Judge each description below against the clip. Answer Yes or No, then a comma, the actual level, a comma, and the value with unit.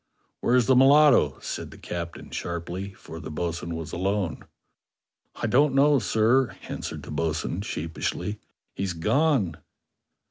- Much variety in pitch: Yes, wide, 7.5 semitones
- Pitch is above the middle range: No, low, 100 Hz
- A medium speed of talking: No, slow, 130 wpm